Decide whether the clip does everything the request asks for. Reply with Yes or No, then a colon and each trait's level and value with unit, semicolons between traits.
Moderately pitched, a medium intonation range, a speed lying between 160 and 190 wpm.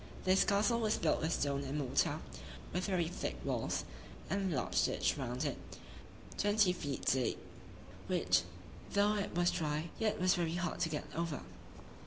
Yes: medium, 170 Hz; average, 4.9 semitones; average, 165 wpm